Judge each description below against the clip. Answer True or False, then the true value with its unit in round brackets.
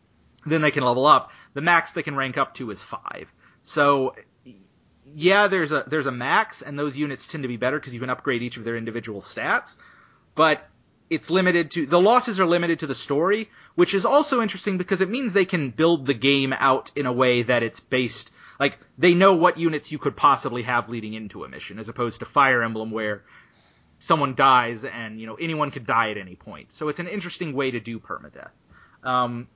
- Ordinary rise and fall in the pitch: False (6.0 semitones)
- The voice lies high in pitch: False (140 Hz)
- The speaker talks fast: True (215 wpm)